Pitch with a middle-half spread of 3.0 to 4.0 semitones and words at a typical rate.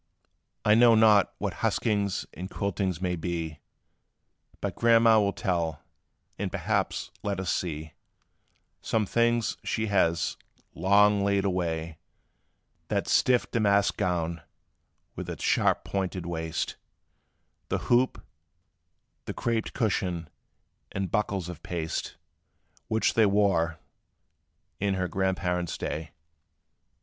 No: average, 3.6 semitones; slow, 110 wpm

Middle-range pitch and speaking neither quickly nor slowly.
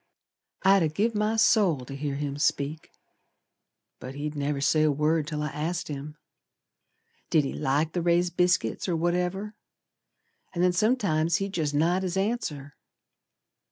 Yes: medium, 160 Hz; average, 155 wpm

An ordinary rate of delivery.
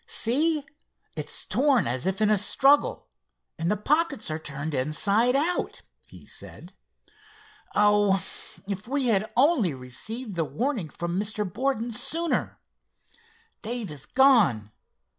No: slow, 125 wpm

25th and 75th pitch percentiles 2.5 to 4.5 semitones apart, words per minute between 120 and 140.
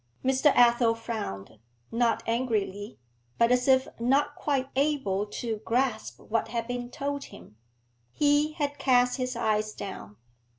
Yes: average, 3.5 semitones; slow, 135 wpm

